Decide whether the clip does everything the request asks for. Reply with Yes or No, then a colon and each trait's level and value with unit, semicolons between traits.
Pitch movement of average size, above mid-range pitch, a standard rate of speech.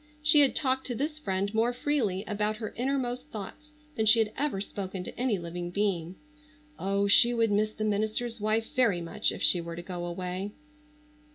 Yes: average, 4.2 semitones; high, 215 Hz; average, 190 wpm